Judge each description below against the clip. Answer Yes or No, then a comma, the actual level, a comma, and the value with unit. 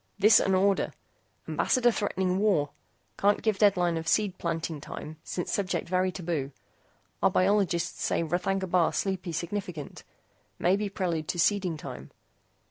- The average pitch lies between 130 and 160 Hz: No, medium, 185 Hz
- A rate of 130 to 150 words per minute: Yes, average, 140 wpm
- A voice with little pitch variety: No, average, 3.0 semitones